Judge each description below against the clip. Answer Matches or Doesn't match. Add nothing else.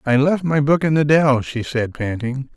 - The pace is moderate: Doesn't match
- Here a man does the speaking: Matches